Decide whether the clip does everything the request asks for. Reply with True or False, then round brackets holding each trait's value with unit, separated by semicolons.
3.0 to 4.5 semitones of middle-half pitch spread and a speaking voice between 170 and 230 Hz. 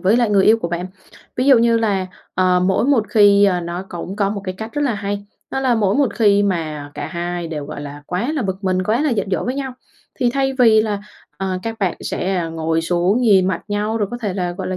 True (4.0 semitones; 200 Hz)